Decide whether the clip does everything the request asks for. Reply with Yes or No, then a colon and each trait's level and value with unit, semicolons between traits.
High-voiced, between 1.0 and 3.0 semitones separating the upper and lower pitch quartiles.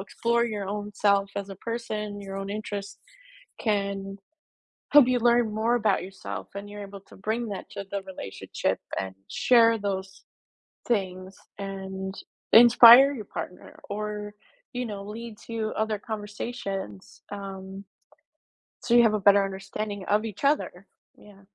Yes: high, 205 Hz; narrow, 2.4 semitones